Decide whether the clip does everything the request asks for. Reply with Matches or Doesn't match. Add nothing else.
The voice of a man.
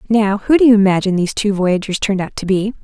Doesn't match